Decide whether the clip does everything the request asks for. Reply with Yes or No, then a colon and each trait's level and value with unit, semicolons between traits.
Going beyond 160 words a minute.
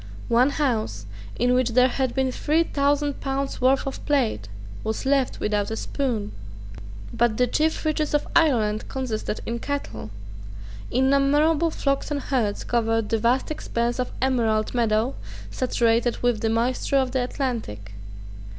No: average, 145 wpm